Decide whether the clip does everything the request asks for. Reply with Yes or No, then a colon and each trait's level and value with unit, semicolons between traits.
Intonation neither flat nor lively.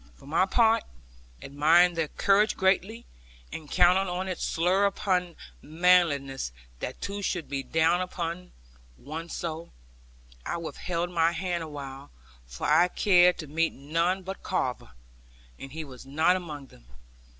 Yes: average, 3.4 semitones